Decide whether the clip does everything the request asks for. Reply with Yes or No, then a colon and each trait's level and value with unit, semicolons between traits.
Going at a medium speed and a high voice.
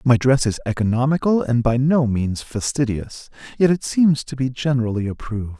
No: average, 170 wpm; low, 125 Hz